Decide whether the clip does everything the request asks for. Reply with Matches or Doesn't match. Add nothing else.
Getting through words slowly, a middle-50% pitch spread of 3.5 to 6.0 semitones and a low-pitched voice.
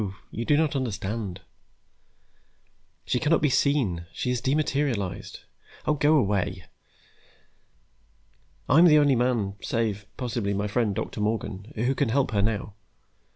Matches